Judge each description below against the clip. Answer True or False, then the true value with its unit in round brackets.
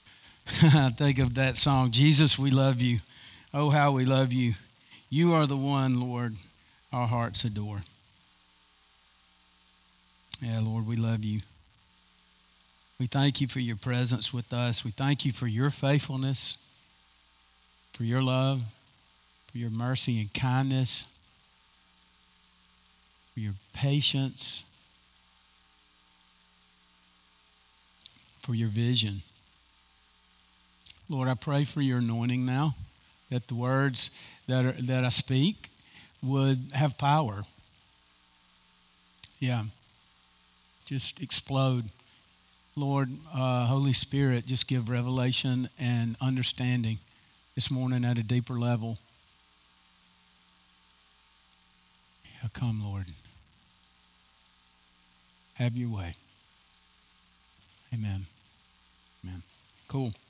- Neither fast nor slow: False (100 wpm)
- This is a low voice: True (110 Hz)